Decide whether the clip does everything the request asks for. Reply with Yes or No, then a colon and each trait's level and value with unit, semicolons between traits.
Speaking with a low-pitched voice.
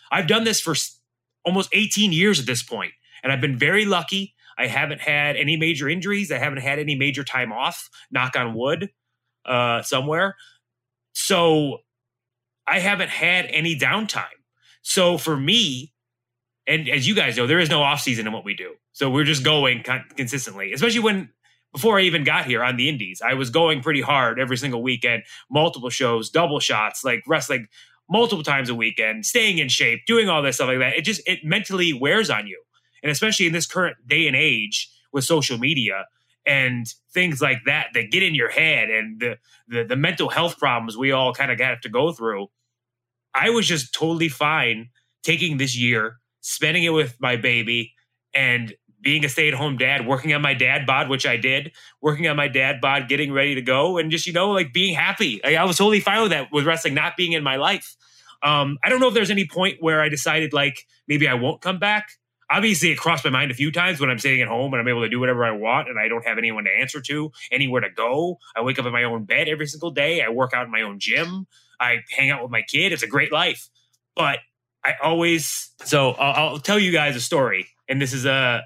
No: medium, 145 Hz